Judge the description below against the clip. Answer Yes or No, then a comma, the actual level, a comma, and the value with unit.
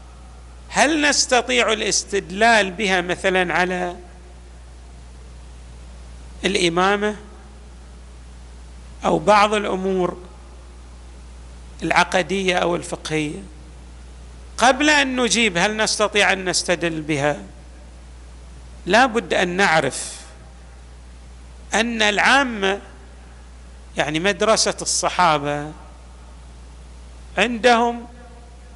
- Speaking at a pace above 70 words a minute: No, slow, 65 wpm